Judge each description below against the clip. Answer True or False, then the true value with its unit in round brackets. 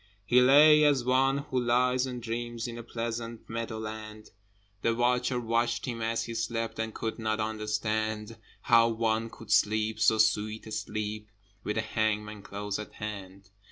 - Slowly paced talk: False (165 wpm)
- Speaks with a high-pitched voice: False (115 Hz)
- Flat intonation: True (1.8 semitones)